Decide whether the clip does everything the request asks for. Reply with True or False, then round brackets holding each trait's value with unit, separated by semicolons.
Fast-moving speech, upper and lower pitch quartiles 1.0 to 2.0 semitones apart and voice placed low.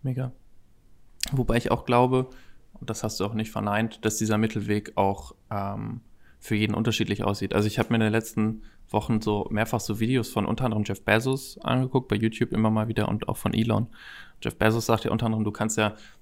True (210 wpm; 1.7 semitones; 110 Hz)